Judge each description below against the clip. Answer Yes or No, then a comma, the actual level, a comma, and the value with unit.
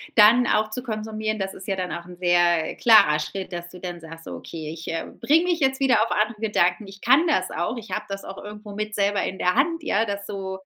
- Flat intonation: No, average, 3.6 semitones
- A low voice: No, high, 205 Hz